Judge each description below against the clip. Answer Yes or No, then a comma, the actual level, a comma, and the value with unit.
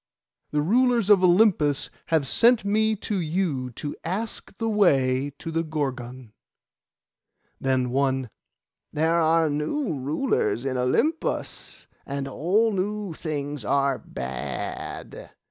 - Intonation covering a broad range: Yes, wide, 7.1 semitones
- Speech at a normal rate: No, slow, 115 wpm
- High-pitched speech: No, medium, 155 Hz